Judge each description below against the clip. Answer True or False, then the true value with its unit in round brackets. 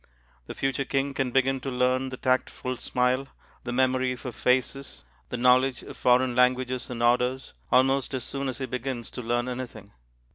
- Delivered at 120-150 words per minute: False (175 wpm)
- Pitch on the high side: False (130 Hz)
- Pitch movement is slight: True (1.1 semitones)